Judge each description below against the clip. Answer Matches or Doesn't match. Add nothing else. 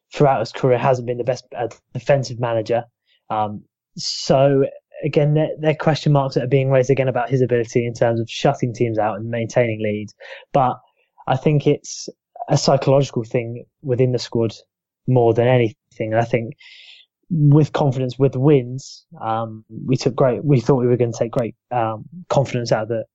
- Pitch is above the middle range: Doesn't match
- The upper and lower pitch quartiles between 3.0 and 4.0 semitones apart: Matches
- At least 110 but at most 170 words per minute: Doesn't match